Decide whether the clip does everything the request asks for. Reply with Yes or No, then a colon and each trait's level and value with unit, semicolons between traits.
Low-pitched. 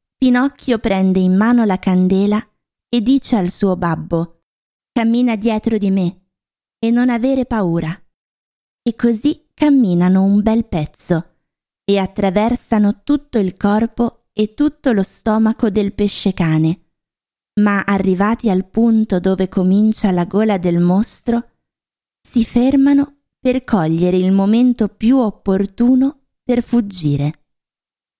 No: high, 210 Hz